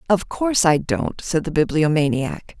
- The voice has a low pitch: No, medium, 165 Hz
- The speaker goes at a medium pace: Yes, average, 160 wpm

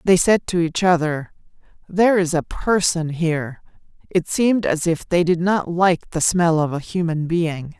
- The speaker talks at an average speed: Yes, average, 185 wpm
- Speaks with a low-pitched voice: No, medium, 170 Hz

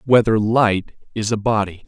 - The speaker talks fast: No, average, 160 wpm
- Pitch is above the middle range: No, low, 110 Hz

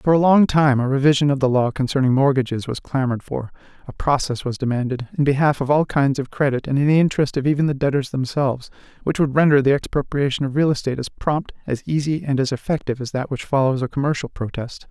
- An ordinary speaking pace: No, fast, 225 wpm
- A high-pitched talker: No, medium, 140 Hz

